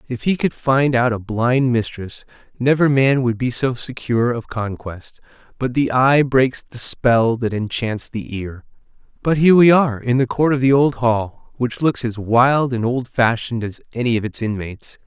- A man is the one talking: Yes, male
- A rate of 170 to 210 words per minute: Yes, average, 185 wpm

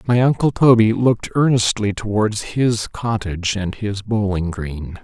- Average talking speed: Yes, average, 145 wpm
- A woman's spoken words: No, male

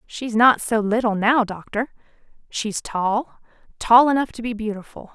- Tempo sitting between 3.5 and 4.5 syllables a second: Yes, 4.4 syllables/s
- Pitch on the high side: Yes, high, 230 Hz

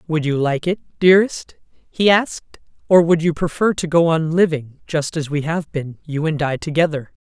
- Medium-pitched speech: Yes, medium, 160 Hz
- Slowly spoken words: No, average, 200 wpm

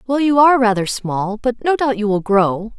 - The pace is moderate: No, fast, 215 wpm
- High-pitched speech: Yes, high, 230 Hz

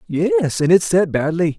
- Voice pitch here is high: No, medium, 160 Hz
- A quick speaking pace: No, average, 190 wpm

